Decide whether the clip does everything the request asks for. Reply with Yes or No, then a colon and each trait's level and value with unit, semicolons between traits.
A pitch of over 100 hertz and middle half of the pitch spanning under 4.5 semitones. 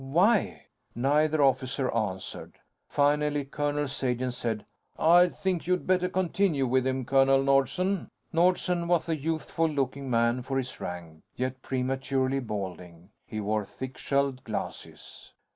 Yes: low, 135 Hz; average, 3.9 semitones